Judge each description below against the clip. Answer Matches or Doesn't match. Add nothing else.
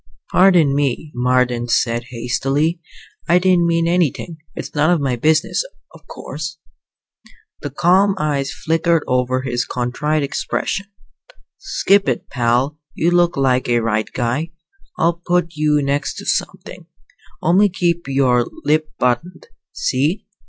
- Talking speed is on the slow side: Matches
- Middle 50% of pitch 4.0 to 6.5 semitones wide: Matches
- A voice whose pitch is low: Doesn't match